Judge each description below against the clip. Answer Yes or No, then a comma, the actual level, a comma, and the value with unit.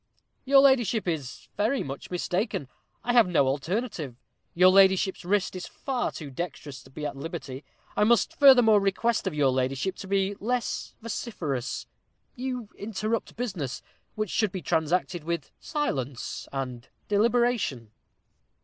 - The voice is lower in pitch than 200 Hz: Yes, high, 190 Hz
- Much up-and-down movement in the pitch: Yes, wide, 7.9 semitones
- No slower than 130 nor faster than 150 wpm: Yes, average, 140 wpm